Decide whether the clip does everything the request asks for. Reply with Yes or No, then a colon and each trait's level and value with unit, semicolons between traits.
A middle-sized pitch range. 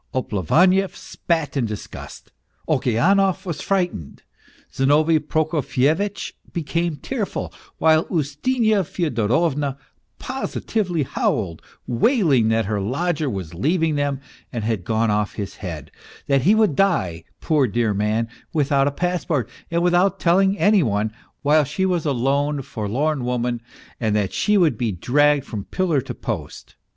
No: wide, 7.2 semitones